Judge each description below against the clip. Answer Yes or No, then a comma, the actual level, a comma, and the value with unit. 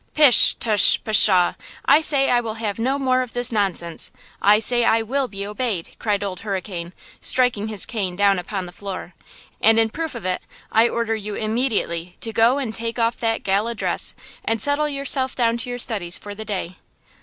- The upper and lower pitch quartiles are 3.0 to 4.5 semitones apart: Yes, average, 3.5 semitones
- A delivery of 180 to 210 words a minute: Yes, average, 195 wpm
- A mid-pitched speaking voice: No, high, 225 Hz